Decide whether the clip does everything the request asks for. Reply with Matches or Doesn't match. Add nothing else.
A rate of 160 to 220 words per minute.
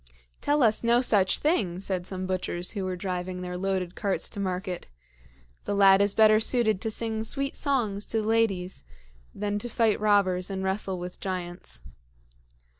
Matches